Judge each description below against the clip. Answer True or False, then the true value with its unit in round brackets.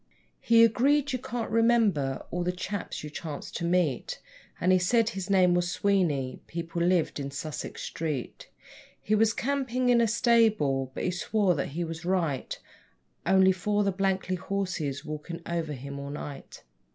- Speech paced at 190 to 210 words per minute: False (165 wpm)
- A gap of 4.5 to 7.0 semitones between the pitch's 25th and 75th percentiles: True (5.6 semitones)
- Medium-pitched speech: True (180 Hz)